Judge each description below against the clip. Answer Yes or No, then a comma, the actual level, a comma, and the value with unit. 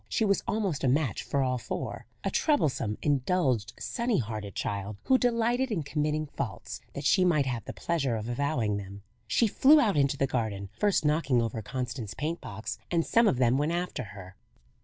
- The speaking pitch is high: No, medium, 140 Hz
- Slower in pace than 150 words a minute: No, average, 190 wpm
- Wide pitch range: Yes, wide, 7.5 semitones